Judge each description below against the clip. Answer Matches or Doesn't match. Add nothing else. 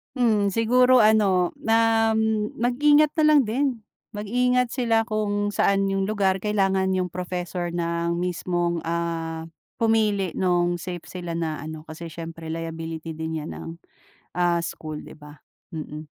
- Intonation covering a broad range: Doesn't match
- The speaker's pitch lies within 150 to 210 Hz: Matches